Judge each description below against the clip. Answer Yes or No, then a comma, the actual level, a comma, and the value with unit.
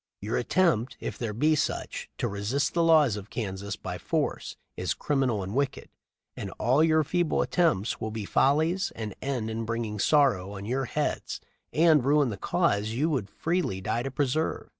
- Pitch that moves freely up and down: Yes, wide, 6.2 semitones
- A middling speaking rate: Yes, average, 180 wpm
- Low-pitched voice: Yes, low, 125 Hz